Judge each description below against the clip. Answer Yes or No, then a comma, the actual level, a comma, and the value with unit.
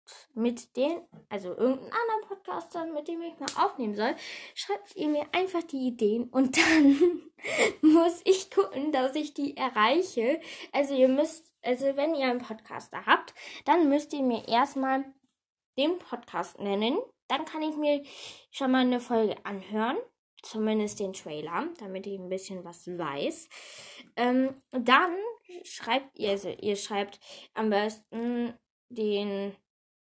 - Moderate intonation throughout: No, wide, 6.2 semitones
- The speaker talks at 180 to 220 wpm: No, average, 145 wpm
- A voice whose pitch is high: Yes, very high, 265 Hz